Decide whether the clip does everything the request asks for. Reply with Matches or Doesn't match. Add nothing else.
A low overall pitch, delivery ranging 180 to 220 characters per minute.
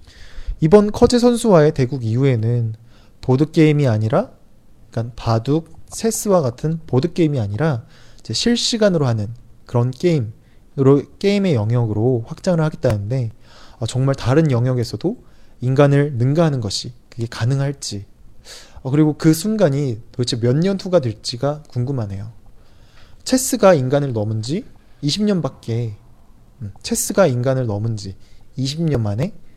Doesn't match